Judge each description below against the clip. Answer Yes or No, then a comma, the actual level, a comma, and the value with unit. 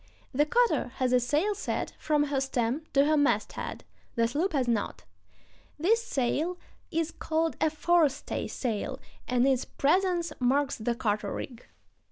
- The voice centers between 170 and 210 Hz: No, very high, 285 Hz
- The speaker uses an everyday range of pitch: Yes, average, 4.8 semitones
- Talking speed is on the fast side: No, average, 150 wpm